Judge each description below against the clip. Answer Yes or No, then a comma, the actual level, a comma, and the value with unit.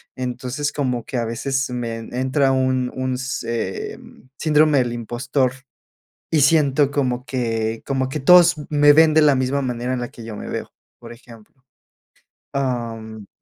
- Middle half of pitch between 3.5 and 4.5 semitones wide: No, average, 2.8 semitones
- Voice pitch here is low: Yes, low, 130 Hz